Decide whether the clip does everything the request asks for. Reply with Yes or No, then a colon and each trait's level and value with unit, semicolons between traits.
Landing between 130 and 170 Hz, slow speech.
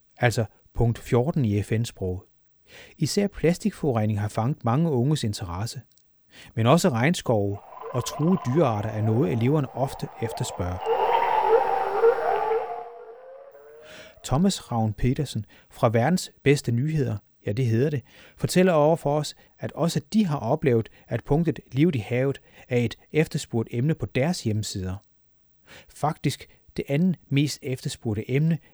Yes: low, 135 Hz; slow, 130 wpm